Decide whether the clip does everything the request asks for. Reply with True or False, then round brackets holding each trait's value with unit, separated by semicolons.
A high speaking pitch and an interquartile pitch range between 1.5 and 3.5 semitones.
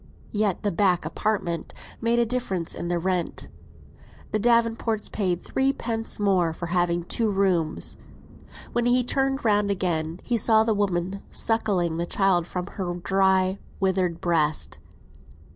False (195 Hz; 4.1 semitones)